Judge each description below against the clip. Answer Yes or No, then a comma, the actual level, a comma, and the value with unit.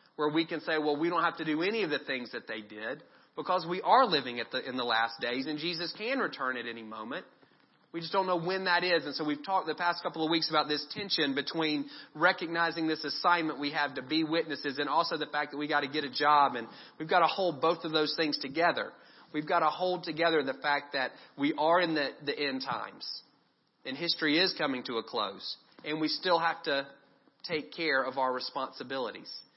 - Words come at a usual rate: No, fast, 235 wpm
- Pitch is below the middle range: No, medium, 155 Hz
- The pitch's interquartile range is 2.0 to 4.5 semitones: Yes, average, 2.9 semitones